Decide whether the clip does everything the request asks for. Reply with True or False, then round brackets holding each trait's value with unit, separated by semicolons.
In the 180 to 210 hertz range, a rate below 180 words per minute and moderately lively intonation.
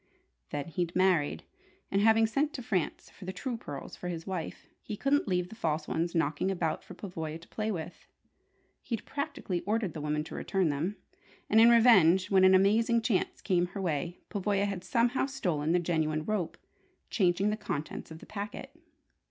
False (185 Hz; 185 wpm; 4.6 semitones)